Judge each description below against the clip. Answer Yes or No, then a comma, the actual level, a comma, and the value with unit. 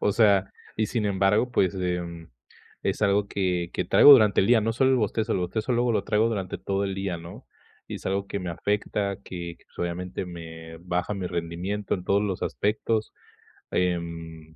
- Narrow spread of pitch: No, average, 3.1 semitones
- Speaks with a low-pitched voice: Yes, very low, 95 Hz